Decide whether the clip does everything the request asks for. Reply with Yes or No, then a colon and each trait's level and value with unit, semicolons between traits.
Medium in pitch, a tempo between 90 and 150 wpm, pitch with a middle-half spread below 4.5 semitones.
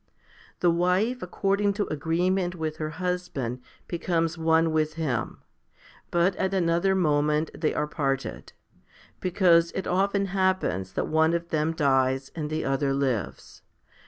Yes: medium, 165 Hz; slow, 135 wpm; average, 3.3 semitones